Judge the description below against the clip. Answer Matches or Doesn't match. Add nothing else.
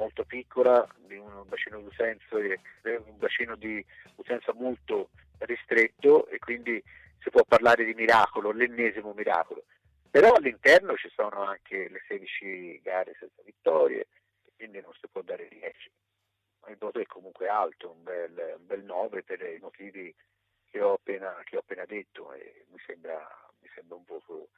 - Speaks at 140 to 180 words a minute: Matches